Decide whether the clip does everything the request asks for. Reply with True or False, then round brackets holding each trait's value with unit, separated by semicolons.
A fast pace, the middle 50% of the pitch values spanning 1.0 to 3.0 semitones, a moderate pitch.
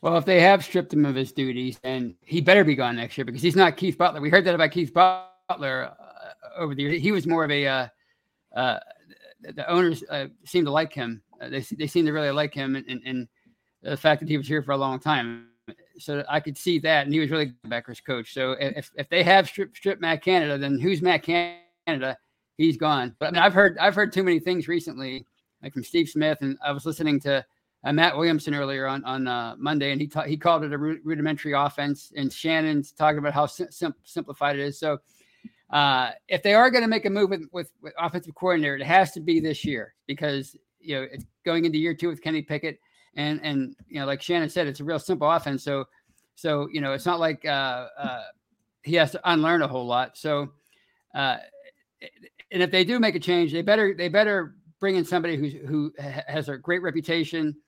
False (230 wpm; 3.7 semitones; 155 Hz)